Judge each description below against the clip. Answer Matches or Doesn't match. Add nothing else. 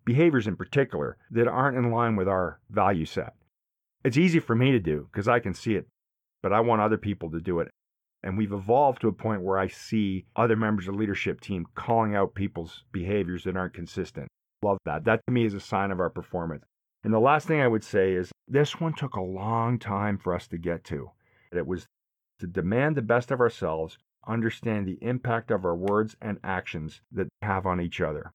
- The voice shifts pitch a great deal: Doesn't match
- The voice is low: Matches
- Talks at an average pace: Doesn't match